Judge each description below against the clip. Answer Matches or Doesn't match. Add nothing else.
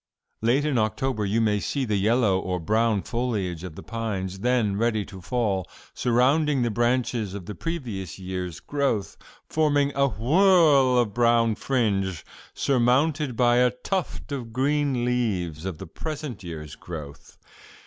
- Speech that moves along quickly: Doesn't match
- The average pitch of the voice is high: Doesn't match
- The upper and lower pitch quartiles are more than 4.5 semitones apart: Matches